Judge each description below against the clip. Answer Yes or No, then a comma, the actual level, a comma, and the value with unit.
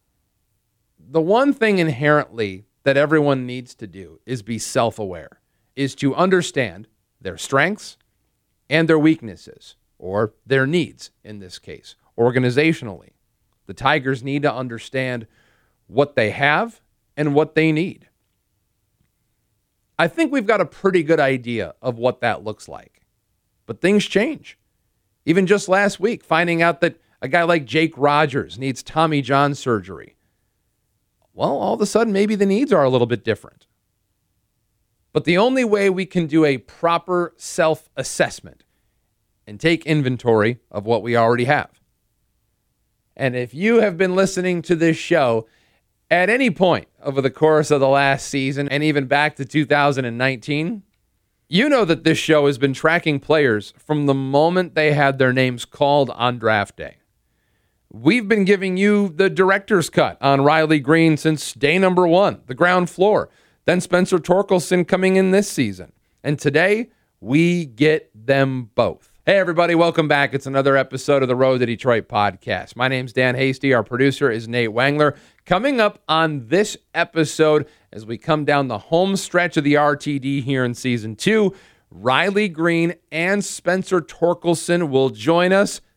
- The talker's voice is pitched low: No, medium, 145 Hz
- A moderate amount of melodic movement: No, wide, 5.9 semitones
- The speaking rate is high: No, average, 160 wpm